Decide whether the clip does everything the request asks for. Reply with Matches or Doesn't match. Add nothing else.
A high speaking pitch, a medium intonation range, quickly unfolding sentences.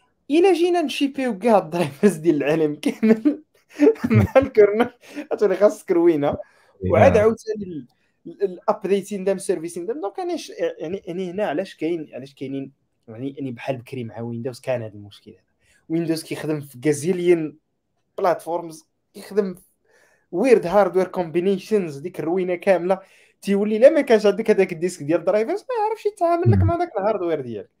Doesn't match